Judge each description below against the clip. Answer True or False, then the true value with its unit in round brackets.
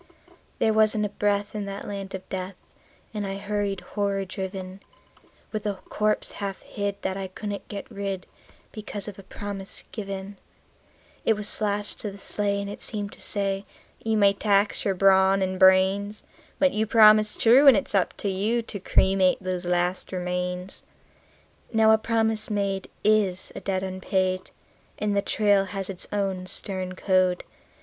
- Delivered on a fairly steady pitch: True (1.7 semitones)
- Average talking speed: True (165 wpm)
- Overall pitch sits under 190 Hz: False (200 Hz)